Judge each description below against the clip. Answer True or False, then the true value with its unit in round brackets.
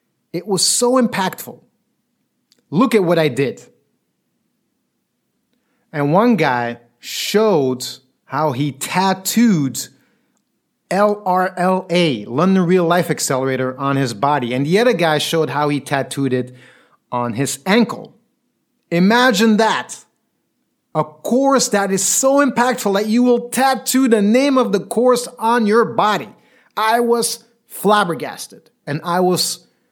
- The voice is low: False (190 Hz)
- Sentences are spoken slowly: True (125 wpm)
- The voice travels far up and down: True (8.0 semitones)